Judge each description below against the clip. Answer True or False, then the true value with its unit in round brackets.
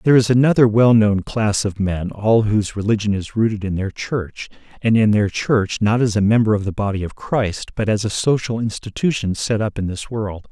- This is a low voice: True (105 Hz)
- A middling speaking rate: False (225 wpm)